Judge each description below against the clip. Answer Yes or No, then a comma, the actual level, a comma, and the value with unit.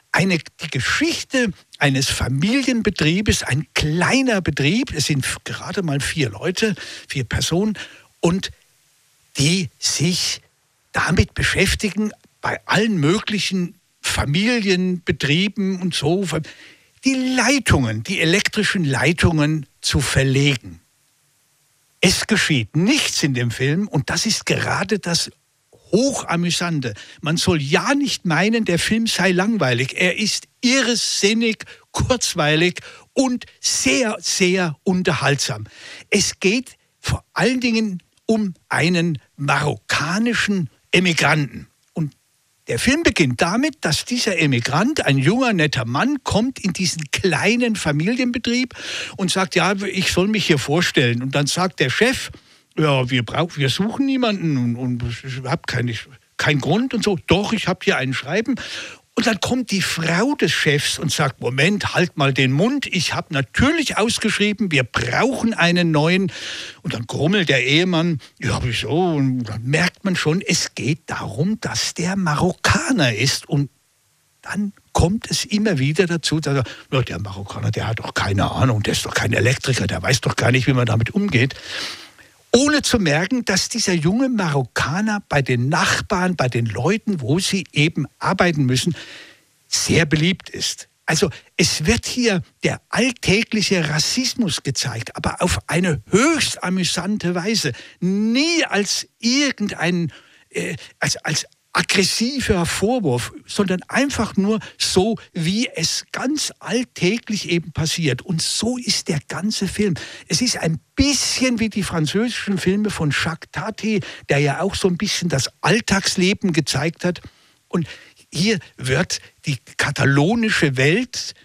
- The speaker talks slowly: No, average, 140 wpm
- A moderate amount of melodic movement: No, wide, 6.6 semitones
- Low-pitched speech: No, medium, 175 Hz